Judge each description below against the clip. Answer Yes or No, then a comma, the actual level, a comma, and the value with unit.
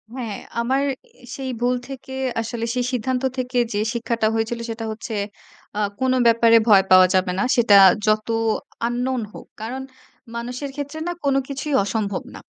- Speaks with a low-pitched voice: No, high, 240 Hz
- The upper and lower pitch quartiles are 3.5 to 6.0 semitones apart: No, average, 2.8 semitones